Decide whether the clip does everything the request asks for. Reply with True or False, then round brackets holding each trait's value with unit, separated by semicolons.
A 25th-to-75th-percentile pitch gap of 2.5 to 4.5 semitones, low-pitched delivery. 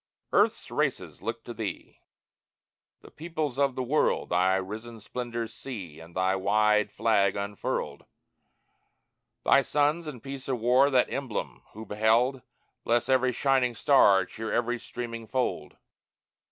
True (3.9 semitones; 115 Hz)